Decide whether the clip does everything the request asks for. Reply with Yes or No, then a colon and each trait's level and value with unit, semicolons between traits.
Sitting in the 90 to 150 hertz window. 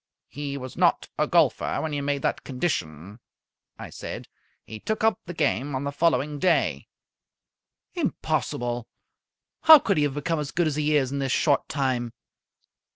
Yes: medium, 140 Hz